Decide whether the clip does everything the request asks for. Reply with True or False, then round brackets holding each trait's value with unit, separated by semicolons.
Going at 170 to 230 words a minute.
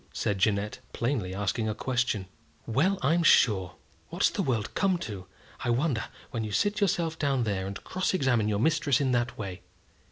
True (180 wpm)